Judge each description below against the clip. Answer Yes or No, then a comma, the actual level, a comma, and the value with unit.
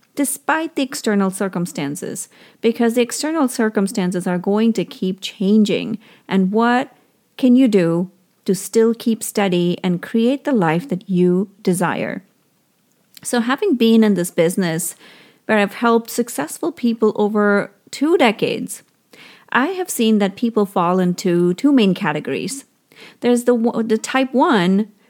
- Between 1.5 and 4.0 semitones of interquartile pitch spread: No, average, 4.4 semitones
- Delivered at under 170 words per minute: Yes, average, 140 wpm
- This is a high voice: Yes, high, 215 Hz